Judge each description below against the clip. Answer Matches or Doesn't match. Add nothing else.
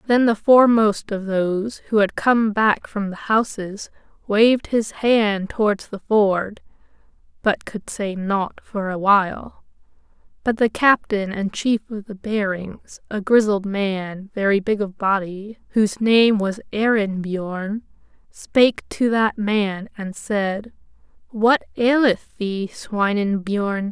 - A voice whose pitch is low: Doesn't match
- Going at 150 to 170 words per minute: Doesn't match